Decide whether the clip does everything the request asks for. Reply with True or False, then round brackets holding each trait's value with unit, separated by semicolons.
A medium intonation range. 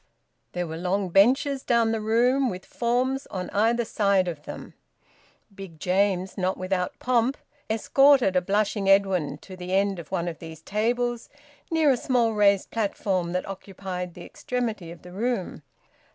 True (4.5 semitones)